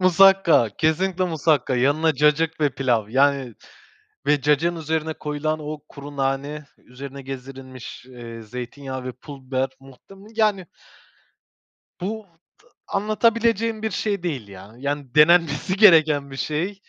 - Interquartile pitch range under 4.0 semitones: No, average, 4.5 semitones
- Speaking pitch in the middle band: Yes, medium, 150 Hz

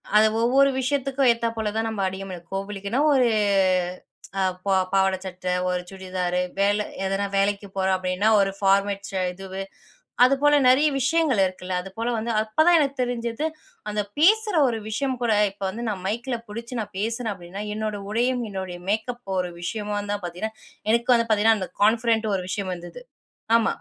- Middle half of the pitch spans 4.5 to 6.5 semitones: No, average, 3.8 semitones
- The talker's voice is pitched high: Yes, high, 215 Hz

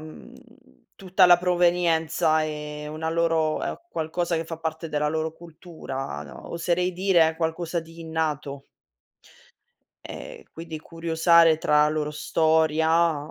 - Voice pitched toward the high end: No, medium, 160 Hz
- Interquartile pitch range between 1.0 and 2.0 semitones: Yes, narrow, 1.5 semitones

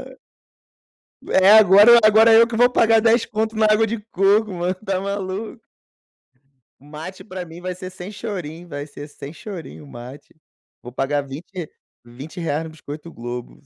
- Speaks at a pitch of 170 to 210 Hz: Yes, medium, 185 Hz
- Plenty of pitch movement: Yes, wide, 6.2 semitones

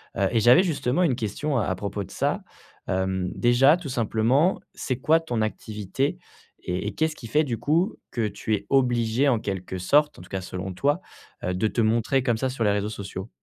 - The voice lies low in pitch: Yes, low, 115 Hz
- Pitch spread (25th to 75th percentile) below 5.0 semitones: No, wide, 5.4 semitones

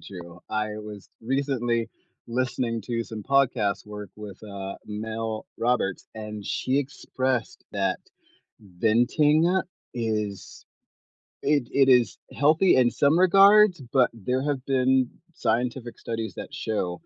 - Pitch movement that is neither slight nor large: Yes, average, 4.0 semitones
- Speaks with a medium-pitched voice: No, low, 120 Hz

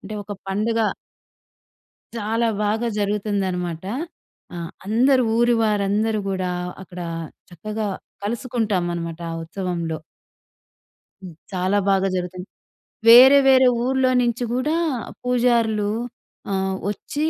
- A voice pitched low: No, high, 210 Hz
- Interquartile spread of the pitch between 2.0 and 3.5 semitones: No, average, 4.1 semitones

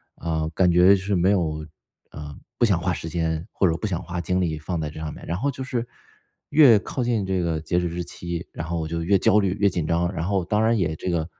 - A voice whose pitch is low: Yes, very low, 85 Hz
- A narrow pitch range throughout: No, average, 3.2 semitones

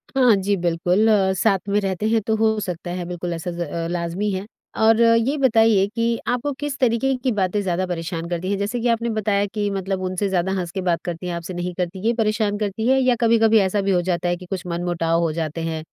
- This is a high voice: Yes, high, 195 Hz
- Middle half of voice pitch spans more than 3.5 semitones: Yes, average, 4.1 semitones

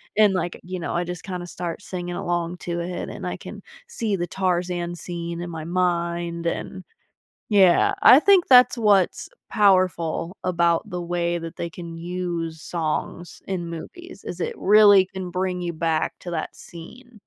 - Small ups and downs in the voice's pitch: Yes, narrow, 1.8 semitones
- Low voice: No, medium, 175 Hz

